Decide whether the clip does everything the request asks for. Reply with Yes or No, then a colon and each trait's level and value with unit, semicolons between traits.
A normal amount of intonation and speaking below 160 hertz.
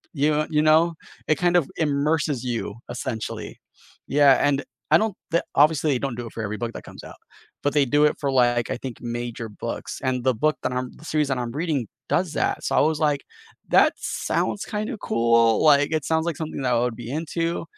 Yes: average, 4.2 semitones; medium, 140 Hz